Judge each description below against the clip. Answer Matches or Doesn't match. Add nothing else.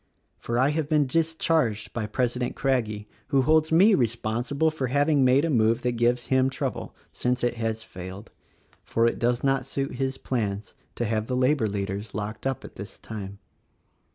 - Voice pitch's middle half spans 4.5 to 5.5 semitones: Doesn't match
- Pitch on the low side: Matches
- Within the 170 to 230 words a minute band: Matches